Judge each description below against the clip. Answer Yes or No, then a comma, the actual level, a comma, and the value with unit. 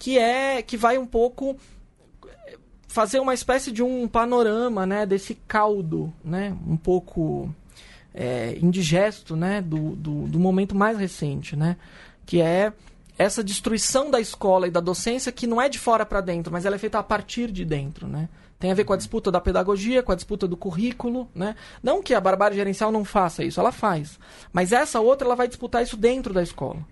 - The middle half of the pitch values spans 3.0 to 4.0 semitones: No, average, 5.0 semitones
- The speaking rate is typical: No, fast, 195 wpm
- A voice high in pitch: Yes, high, 205 Hz